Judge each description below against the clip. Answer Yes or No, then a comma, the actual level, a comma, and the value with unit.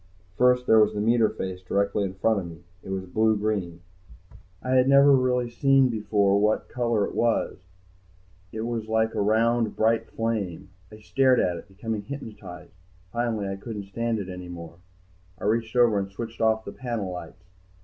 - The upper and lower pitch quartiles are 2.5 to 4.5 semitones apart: Yes, average, 3.1 semitones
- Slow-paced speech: No, average, 180 wpm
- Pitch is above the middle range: No, low, 110 Hz